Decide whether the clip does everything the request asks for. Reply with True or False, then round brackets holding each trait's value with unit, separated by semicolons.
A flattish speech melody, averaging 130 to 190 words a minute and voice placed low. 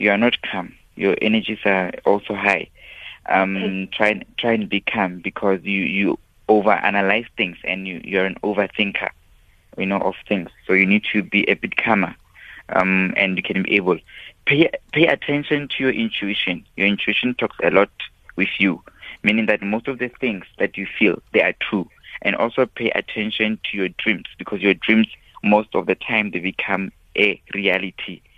True (2.3 semitones; 185 wpm; 105 Hz)